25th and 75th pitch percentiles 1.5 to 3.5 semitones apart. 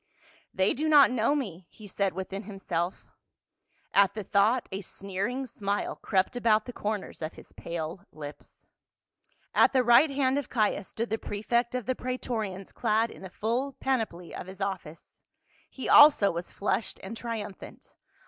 No: average, 4.4 semitones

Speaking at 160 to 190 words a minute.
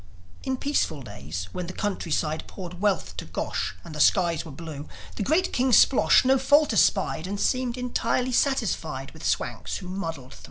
Yes: average, 175 wpm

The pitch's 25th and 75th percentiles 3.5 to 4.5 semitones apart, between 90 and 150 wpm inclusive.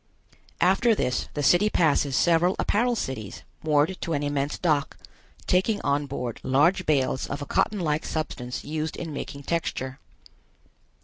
Yes: average, 4.0 semitones; average, 145 wpm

